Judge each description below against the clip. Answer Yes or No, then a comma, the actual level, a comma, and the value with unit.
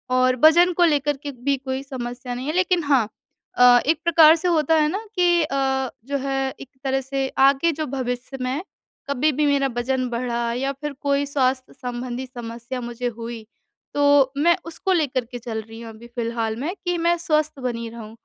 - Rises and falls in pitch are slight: No, average, 3.7 semitones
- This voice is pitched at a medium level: No, very high, 270 Hz